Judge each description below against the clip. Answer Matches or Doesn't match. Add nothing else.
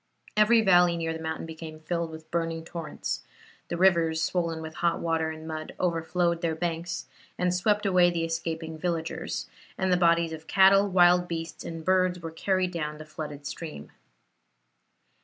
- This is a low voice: Doesn't match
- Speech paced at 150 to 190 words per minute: Matches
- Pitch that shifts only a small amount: Matches